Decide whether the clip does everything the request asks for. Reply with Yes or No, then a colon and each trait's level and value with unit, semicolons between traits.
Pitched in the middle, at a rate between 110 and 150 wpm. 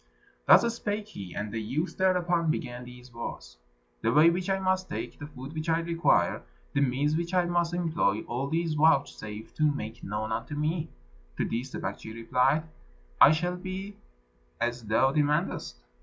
No: medium, 150 Hz; average, 170 wpm